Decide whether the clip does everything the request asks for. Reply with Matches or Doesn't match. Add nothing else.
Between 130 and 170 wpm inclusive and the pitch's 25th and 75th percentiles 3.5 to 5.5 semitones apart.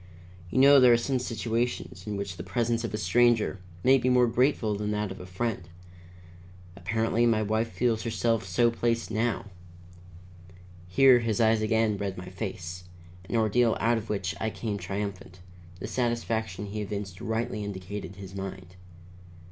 Doesn't match